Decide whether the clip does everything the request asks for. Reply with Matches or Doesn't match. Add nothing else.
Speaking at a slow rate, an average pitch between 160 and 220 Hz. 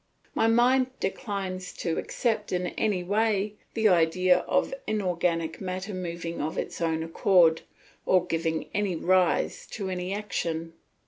Matches